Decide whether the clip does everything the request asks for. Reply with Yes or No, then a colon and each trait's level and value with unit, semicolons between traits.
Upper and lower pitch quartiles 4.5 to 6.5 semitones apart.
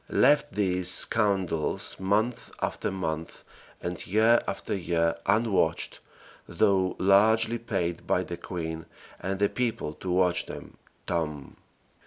No: average, 3.8 semitones